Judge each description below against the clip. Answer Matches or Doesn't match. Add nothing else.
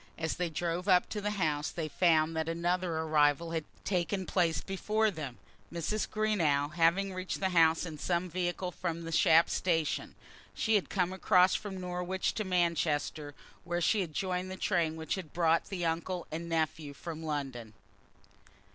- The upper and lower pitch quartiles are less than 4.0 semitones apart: Matches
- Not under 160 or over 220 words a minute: Matches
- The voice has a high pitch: Doesn't match